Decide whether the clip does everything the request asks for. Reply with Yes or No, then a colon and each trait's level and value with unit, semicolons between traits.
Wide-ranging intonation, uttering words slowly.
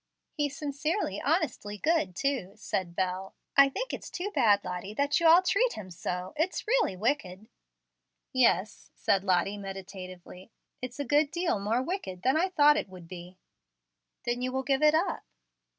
No: wide, 8.2 semitones; average, 165 wpm